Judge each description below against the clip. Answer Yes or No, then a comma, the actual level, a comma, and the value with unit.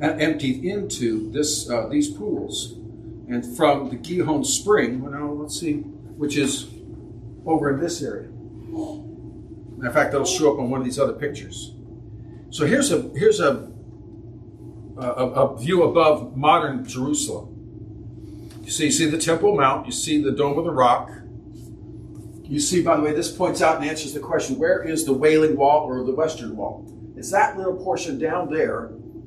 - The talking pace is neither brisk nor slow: Yes, average, 170 wpm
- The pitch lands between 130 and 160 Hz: Yes, medium, 140 Hz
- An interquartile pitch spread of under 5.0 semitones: No, wide, 5.4 semitones